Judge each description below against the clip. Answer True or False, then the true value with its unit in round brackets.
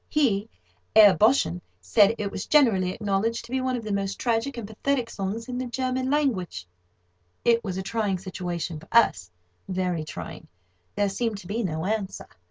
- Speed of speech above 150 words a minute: True (175 wpm)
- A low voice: False (205 Hz)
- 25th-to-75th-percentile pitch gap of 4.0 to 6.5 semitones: True (4.3 semitones)